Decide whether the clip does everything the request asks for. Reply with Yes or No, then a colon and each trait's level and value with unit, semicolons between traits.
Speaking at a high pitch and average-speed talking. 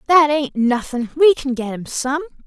Yes: very high, 275 Hz; average, 195 wpm